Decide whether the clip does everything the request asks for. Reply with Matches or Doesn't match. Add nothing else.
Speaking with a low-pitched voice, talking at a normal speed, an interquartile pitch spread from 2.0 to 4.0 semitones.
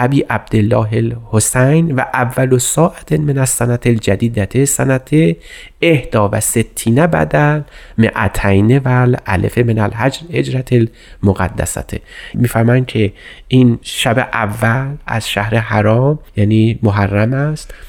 Matches